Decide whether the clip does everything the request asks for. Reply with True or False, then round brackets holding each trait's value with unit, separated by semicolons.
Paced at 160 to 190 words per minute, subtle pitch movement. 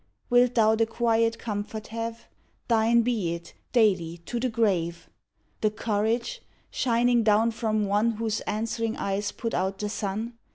False (150 wpm; 2.0 semitones)